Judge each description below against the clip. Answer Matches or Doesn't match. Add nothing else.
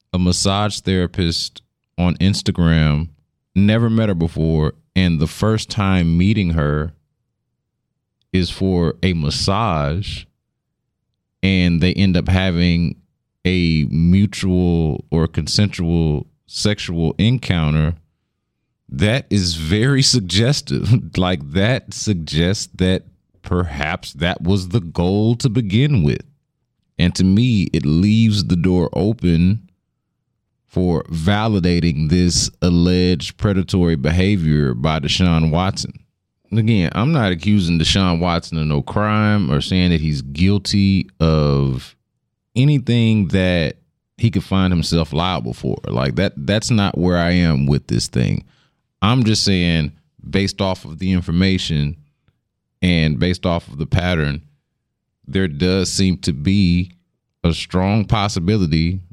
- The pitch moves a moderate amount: Matches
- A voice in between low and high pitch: Doesn't match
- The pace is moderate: Doesn't match